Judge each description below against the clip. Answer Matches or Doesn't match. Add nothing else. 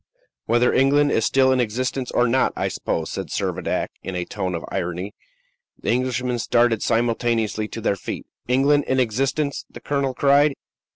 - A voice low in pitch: Matches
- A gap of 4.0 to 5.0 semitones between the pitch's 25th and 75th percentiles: Doesn't match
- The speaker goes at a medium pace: Matches